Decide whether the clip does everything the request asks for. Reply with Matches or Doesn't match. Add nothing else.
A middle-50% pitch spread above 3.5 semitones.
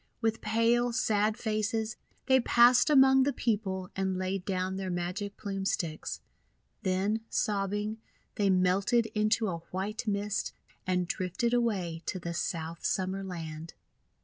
Doesn't match